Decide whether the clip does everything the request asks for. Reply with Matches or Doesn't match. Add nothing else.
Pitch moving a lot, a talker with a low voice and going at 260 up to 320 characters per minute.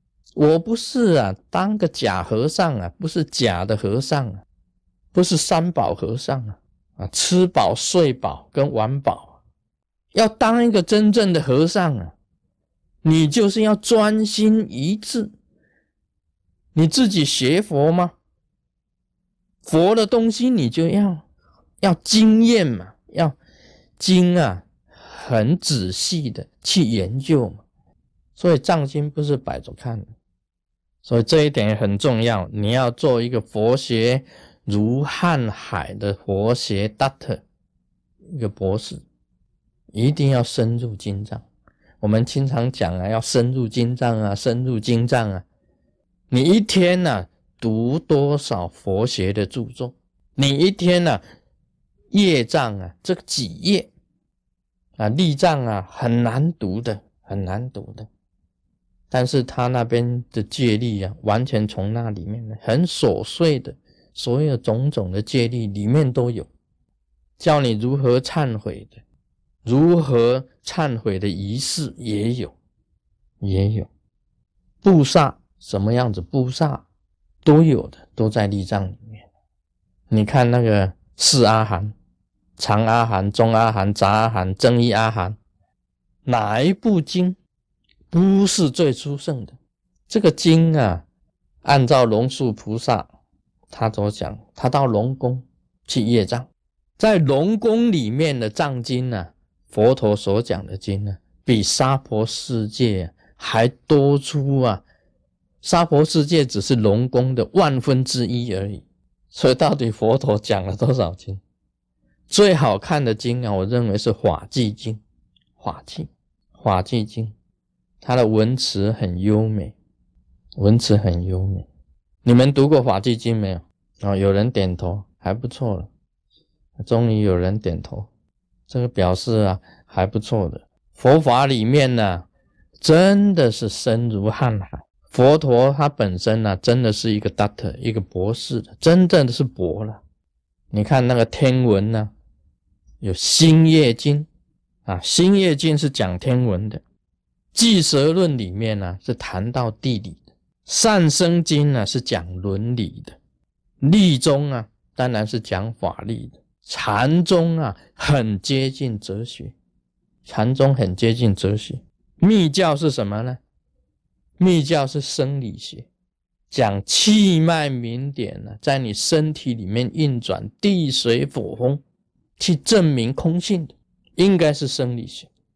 Doesn't match